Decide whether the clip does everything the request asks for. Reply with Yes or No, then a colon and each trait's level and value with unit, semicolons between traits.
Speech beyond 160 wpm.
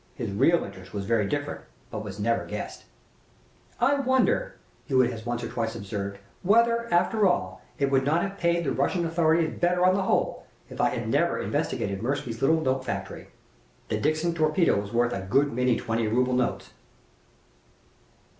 Yes: average, 175 wpm